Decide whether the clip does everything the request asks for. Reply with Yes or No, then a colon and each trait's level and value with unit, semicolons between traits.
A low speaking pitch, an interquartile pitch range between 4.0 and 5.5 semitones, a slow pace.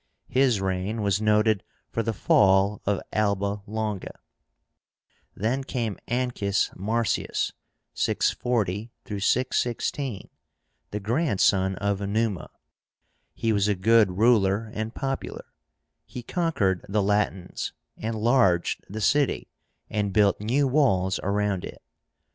No: low, 105 Hz; average, 2.8 semitones; slow, 105 wpm